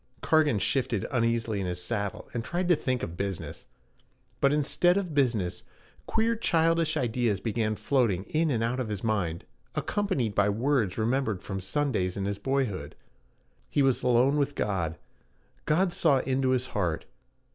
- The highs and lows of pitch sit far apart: Yes, wide, 6.0 semitones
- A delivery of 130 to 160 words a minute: Yes, average, 155 wpm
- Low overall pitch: Yes, low, 120 Hz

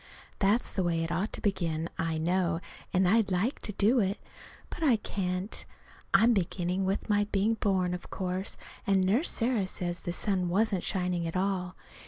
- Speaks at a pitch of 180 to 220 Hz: Yes, high, 190 Hz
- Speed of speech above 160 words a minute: Yes, average, 180 wpm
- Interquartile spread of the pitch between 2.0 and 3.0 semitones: Yes, narrow, 2.5 semitones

